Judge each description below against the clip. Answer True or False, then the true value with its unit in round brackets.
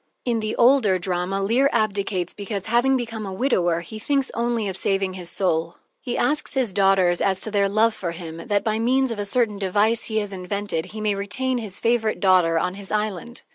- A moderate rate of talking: False (210 wpm)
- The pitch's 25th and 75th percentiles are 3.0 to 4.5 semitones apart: True (3.5 semitones)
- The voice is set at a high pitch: True (205 Hz)